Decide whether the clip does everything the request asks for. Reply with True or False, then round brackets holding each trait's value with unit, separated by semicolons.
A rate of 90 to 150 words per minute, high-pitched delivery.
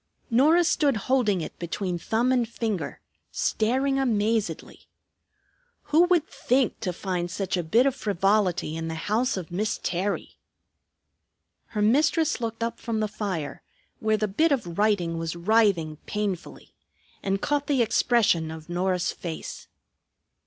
True (140 wpm; 210 Hz)